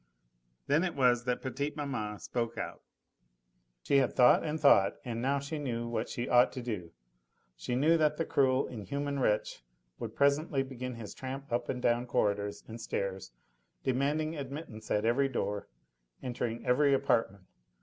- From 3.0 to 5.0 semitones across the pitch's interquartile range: Yes, average, 3.4 semitones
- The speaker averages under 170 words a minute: Yes, average, 160 wpm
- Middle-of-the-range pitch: No, low, 125 Hz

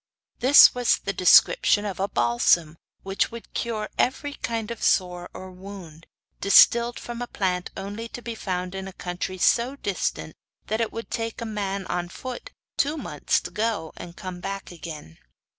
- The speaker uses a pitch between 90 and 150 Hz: No, high, 195 Hz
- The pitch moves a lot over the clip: No, average, 4.4 semitones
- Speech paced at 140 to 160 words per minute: No, average, 175 wpm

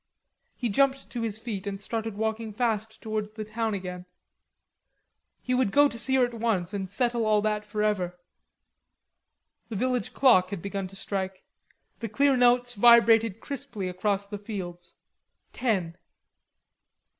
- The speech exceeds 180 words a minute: No, average, 145 wpm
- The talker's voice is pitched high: Yes, high, 215 Hz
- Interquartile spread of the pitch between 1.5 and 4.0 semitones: Yes, average, 3.1 semitones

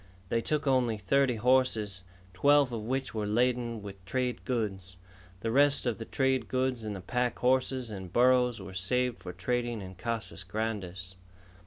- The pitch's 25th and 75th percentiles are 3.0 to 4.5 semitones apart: Yes, average, 4.2 semitones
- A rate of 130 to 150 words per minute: No, average, 165 wpm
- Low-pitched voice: Yes, low, 115 Hz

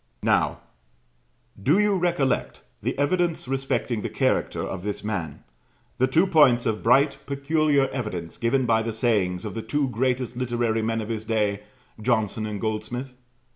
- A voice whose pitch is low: Yes, low, 120 Hz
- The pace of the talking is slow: No, average, 155 wpm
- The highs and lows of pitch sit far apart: No, average, 4.1 semitones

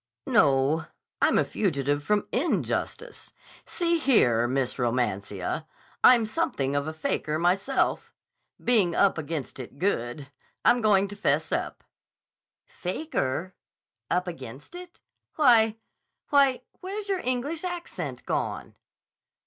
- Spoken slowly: Yes, slow, 110 wpm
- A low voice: No, medium, 185 Hz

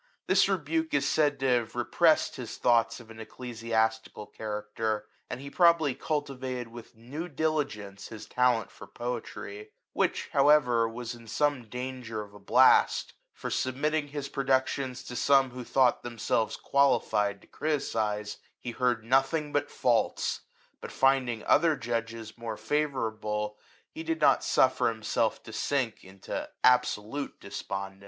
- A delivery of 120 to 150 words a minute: Yes, average, 145 wpm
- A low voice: Yes, low, 125 Hz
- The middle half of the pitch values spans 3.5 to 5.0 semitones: Yes, average, 4.0 semitones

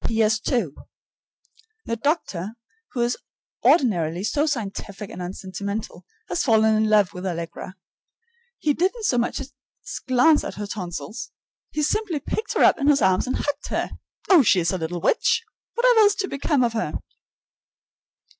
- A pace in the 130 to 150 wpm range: No, average, 160 wpm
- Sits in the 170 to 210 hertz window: No, high, 230 Hz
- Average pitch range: No, wide, 7.4 semitones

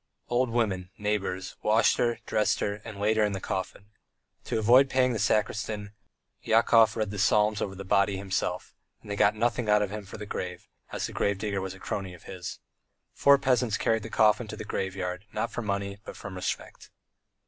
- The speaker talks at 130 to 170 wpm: No, fast, 205 wpm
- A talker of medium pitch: No, low, 105 Hz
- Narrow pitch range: Yes, narrow, 2.1 semitones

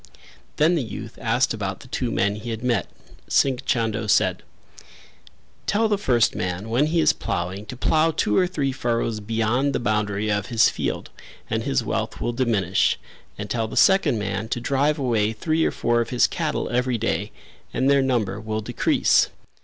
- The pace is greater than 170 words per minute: Yes, average, 185 wpm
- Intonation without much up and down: No, average, 4.2 semitones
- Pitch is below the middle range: Yes, low, 115 Hz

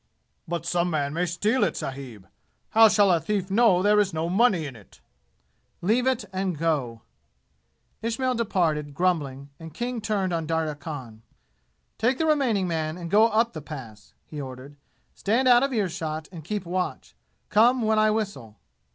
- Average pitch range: No, wide, 6.0 semitones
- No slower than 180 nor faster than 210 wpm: No, average, 170 wpm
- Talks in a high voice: No, medium, 180 Hz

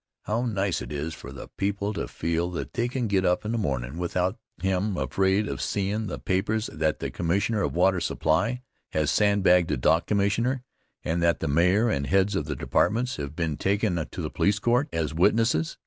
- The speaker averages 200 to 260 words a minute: Yes, fast, 205 wpm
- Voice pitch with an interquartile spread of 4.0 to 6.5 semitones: Yes, average, 4.3 semitones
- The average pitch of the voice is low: Yes, very low, 95 Hz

